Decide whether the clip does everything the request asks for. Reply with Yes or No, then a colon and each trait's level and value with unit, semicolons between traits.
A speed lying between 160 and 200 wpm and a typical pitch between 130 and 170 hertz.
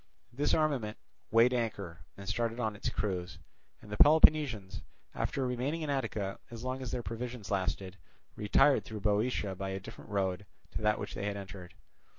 No: average, 175 wpm; low, 110 Hz